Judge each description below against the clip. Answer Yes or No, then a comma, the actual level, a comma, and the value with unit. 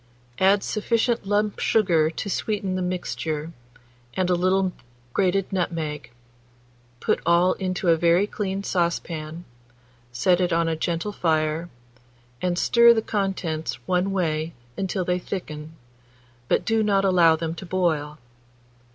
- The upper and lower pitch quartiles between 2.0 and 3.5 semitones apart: Yes, average, 3.1 semitones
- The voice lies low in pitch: No, medium, 180 Hz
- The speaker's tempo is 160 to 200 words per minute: No, slow, 135 wpm